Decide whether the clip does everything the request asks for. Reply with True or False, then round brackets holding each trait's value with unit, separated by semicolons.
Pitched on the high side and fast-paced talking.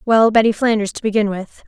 True (215 Hz; 215 wpm)